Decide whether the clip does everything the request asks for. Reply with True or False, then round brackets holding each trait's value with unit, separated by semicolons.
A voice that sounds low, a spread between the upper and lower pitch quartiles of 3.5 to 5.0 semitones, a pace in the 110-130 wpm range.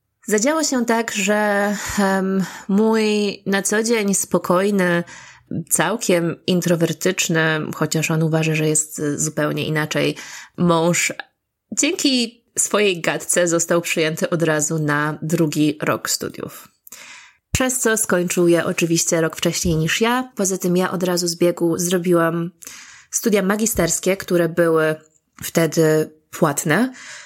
False (175 Hz; 3.9 semitones; 120 wpm)